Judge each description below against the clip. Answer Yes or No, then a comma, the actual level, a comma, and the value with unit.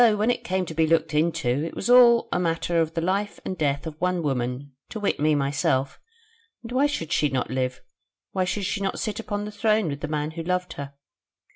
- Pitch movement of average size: No, wide, 5.8 semitones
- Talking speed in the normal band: No, fast, 230 wpm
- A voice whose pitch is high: No, medium, 165 Hz